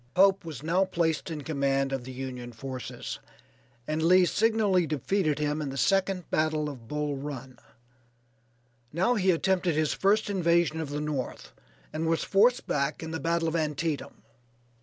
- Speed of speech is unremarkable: Yes, average, 160 wpm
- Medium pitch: Yes, medium, 160 Hz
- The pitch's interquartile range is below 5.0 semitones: Yes, average, 4.1 semitones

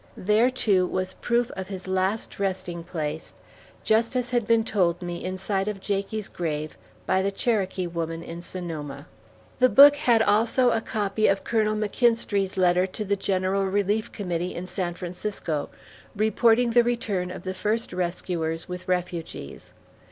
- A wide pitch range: No, average, 3.4 semitones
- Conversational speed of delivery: Yes, average, 160 wpm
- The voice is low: No, high, 190 Hz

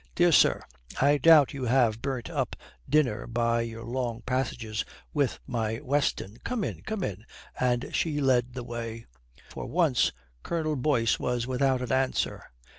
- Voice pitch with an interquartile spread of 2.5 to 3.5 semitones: Yes, average, 3.2 semitones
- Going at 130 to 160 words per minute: Yes, average, 155 wpm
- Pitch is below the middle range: Yes, low, 125 Hz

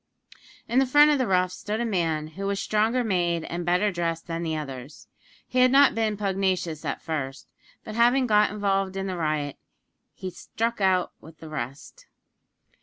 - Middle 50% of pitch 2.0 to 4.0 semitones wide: No, average, 5.0 semitones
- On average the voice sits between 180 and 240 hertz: Yes, high, 190 Hz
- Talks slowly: No, average, 180 wpm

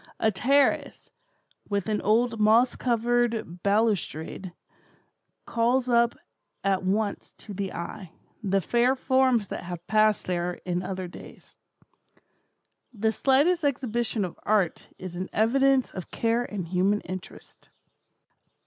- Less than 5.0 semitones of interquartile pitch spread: Yes, average, 4.3 semitones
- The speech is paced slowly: Yes, slow, 120 wpm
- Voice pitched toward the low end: No, high, 215 Hz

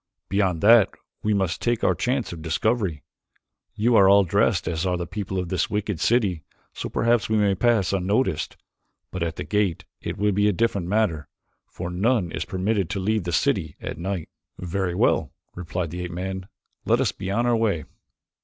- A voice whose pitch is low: Yes, very low, 95 Hz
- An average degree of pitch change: Yes, average, 3.4 semitones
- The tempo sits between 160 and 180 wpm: No, average, 190 wpm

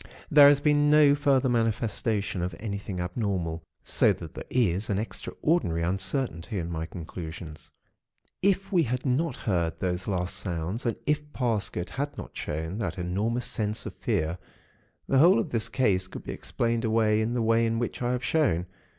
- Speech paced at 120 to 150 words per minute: No, average, 175 wpm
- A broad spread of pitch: Yes, wide, 6.2 semitones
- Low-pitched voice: Yes, low, 110 Hz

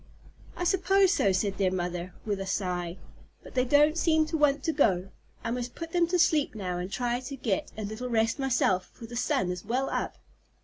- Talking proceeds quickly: Yes, fast, 215 wpm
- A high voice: Yes, high, 240 Hz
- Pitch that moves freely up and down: Yes, wide, 7.6 semitones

